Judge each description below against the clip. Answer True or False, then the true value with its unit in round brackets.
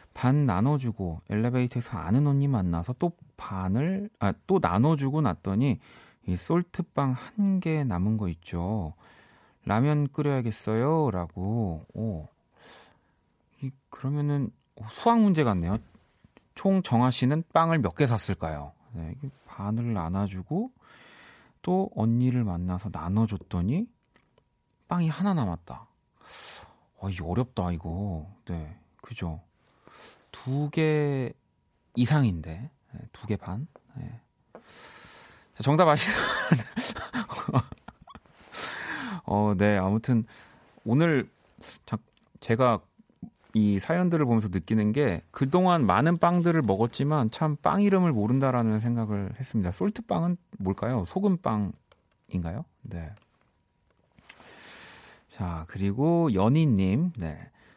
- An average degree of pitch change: False (7.1 semitones)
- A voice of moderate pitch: False (115 Hz)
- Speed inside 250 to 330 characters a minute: False (210 characters per minute)